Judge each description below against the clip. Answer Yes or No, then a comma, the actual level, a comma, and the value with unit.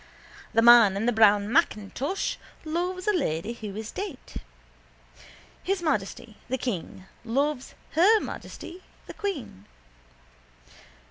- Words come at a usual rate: No, slow, 115 wpm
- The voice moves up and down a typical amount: No, wide, 8.4 semitones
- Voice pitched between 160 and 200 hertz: No, high, 245 Hz